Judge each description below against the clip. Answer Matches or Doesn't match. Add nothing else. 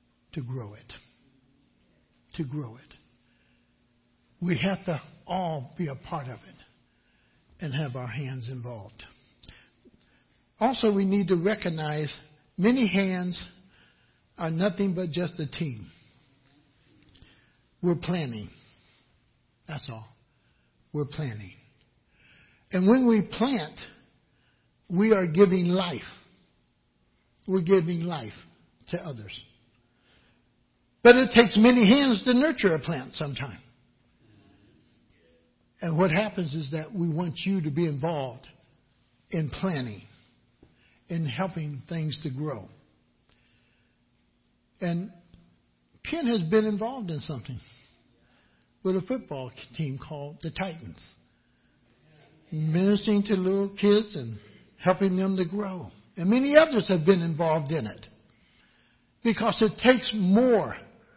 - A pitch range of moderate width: Doesn't match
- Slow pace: Matches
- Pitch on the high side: Doesn't match